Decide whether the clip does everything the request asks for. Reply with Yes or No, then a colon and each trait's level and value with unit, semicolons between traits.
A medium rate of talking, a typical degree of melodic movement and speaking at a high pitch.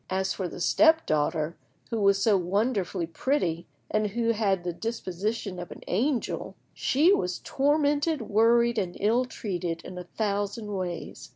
Yes: average, 155 wpm; average, 4.7 semitones; high, 205 Hz